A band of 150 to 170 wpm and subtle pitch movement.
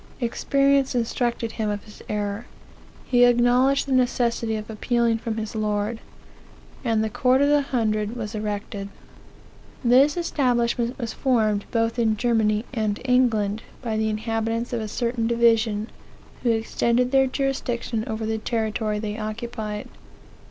No: average, 140 wpm; narrow, 2.2 semitones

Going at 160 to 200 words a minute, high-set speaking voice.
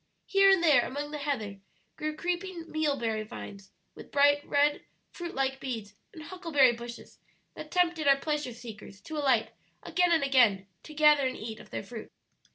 Yes: average, 170 wpm; very high, 285 Hz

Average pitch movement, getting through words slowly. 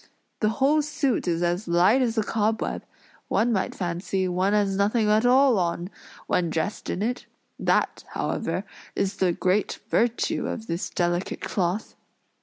No: average, 4.1 semitones; average, 155 wpm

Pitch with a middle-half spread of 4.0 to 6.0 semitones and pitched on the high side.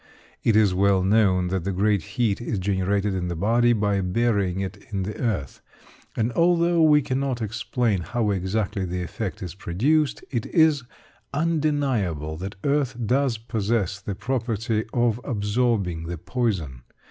No: average, 4.3 semitones; low, 105 Hz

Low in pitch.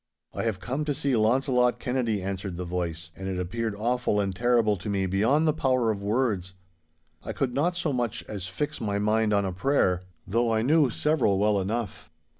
Yes: low, 110 Hz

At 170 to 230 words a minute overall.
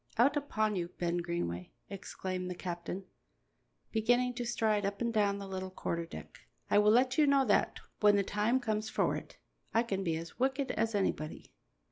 Yes: average, 185 wpm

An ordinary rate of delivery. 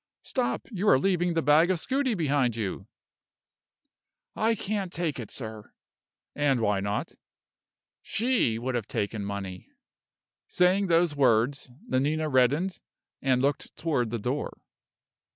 No: slow, 130 wpm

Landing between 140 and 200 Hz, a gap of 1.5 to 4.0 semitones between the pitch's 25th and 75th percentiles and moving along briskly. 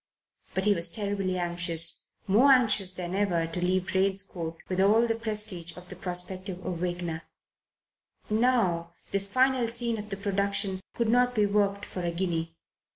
No: high, 190 Hz; average, 3.1 semitones; average, 160 wpm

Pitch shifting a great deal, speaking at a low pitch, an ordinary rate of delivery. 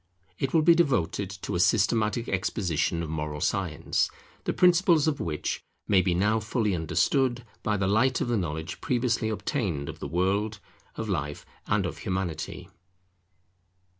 Yes: wide, 5.7 semitones; low, 105 Hz; average, 155 wpm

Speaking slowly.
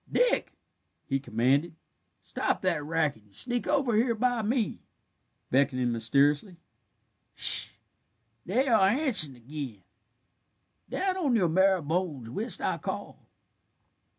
Yes: slow, 125 wpm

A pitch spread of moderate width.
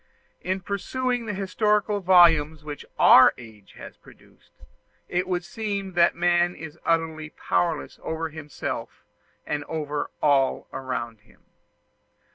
Yes: average, 4.0 semitones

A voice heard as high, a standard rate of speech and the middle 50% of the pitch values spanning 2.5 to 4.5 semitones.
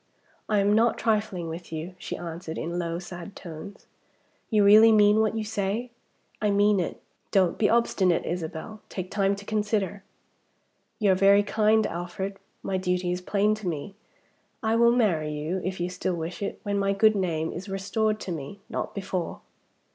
Yes: high, 195 Hz; average, 180 wpm; average, 3.1 semitones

